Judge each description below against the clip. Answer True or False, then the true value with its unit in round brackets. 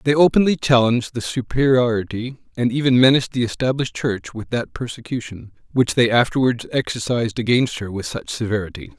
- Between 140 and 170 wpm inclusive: True (155 wpm)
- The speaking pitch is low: True (120 Hz)